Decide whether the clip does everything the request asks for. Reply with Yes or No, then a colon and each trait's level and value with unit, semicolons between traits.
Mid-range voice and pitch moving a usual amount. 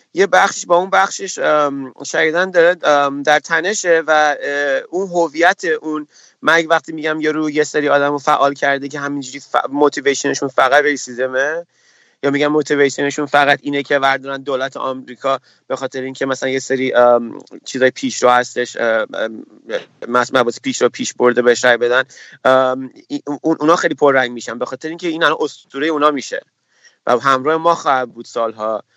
Yes: medium, 145 Hz; average, 3.4 semitones